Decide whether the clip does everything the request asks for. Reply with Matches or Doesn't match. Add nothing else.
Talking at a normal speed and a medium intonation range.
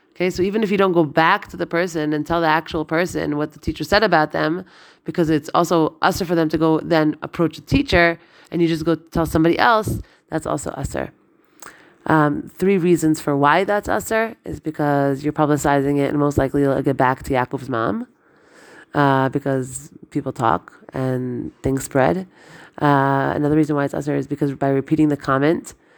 Matches